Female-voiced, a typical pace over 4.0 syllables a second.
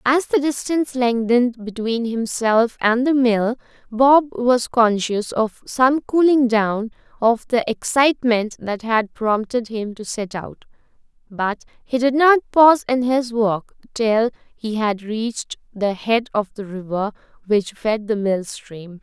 No: female; 3.9 syllables/s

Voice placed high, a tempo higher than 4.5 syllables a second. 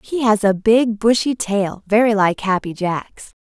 No: high, 210 Hz; 4.1 syllables/s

